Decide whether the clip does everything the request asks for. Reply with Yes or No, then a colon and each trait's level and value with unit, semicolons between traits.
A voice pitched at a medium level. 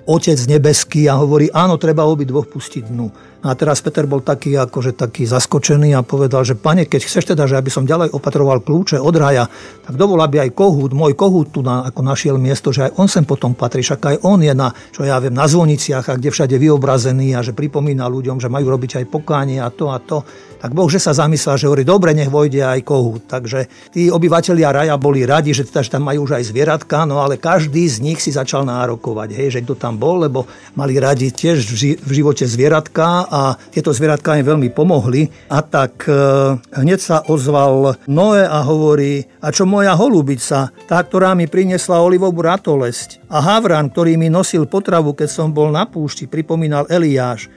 Yes: medium, 145 Hz